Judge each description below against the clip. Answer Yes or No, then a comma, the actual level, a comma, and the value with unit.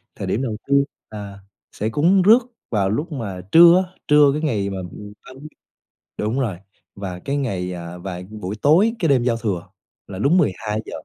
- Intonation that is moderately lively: No, wide, 7.0 semitones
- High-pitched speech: No, low, 115 Hz